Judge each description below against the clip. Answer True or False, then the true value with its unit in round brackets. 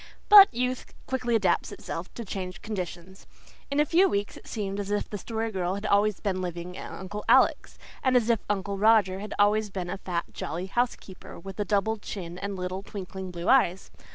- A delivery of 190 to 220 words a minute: True (200 wpm)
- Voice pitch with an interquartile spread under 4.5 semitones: True (3.0 semitones)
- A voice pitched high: True (200 Hz)